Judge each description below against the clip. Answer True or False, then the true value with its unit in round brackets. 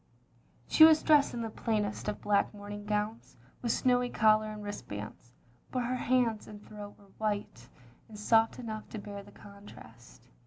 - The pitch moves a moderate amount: False (2.1 semitones)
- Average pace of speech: True (170 wpm)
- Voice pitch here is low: False (210 Hz)